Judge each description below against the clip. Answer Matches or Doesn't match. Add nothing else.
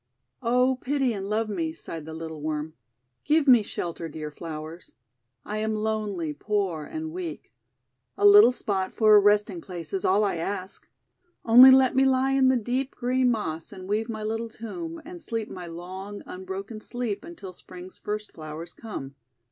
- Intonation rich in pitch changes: Matches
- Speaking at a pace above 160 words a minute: Matches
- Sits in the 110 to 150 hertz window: Doesn't match